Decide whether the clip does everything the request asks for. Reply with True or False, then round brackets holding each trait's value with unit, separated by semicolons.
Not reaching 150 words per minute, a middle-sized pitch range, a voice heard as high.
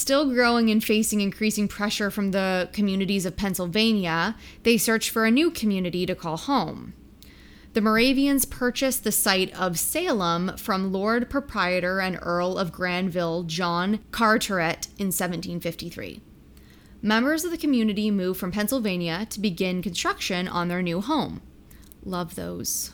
True (140 wpm; 3.7 semitones; 200 Hz)